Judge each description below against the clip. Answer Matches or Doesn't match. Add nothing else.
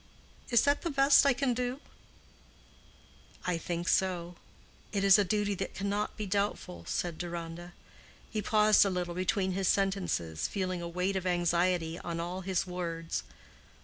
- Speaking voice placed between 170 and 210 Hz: Matches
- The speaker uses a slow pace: Doesn't match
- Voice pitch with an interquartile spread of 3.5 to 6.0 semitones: Doesn't match